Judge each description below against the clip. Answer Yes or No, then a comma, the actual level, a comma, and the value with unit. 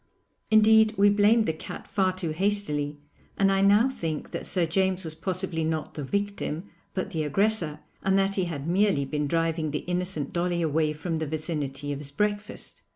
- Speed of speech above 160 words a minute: Yes, average, 185 wpm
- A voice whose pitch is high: No, medium, 175 Hz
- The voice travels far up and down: No, average, 4.3 semitones